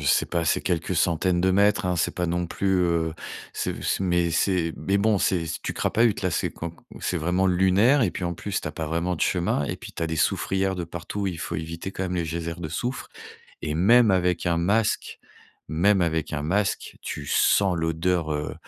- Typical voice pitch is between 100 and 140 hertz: No, very low, 90 Hz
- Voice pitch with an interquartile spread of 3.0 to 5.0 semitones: No, narrow, 2.6 semitones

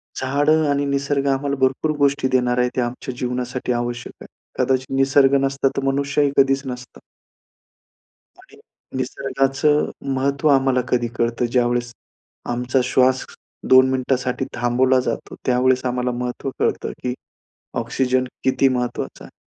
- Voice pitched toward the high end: No, low, 130 Hz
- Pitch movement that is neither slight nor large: No, narrow, 1.7 semitones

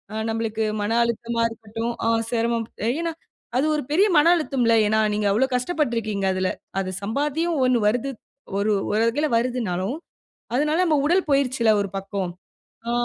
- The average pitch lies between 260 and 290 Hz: No, high, 235 Hz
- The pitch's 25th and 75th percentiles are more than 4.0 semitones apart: Yes, average, 4.6 semitones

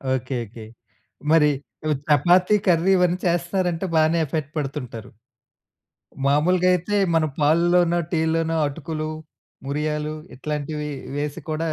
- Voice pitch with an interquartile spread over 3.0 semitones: No, average, 2.7 semitones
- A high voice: No, medium, 160 Hz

